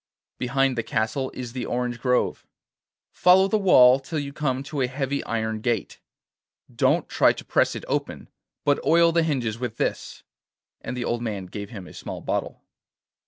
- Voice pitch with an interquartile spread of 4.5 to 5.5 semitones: No, average, 3.3 semitones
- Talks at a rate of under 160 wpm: No, average, 175 wpm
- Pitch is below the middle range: Yes, low, 125 Hz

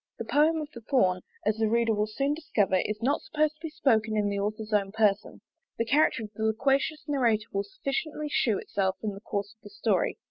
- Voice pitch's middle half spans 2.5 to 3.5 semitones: No, average, 5.1 semitones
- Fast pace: Yes, fast, 220 wpm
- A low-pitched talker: No, high, 220 Hz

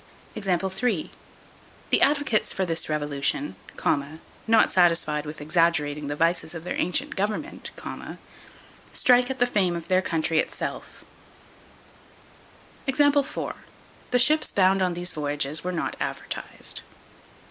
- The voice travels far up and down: Yes, wide, 6.0 semitones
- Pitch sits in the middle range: Yes, medium, 180 Hz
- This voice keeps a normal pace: No, slow, 110 wpm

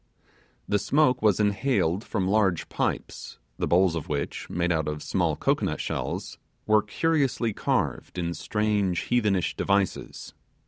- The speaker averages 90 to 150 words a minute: Yes, slow, 135 wpm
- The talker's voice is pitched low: Yes, low, 100 Hz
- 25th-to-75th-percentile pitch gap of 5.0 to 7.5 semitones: No, average, 3.7 semitones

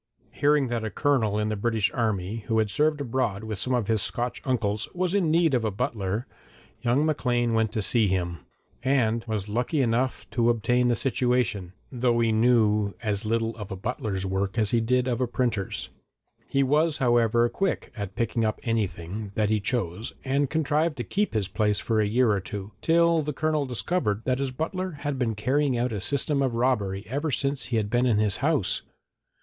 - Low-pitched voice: Yes, low, 120 Hz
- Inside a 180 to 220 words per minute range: Yes, average, 200 wpm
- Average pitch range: Yes, average, 3.8 semitones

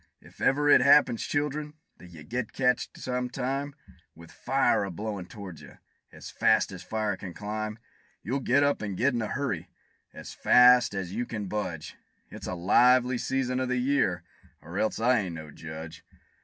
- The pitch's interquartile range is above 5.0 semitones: Yes, wide, 5.6 semitones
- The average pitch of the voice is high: No, low, 115 Hz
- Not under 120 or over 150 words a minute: No, average, 185 wpm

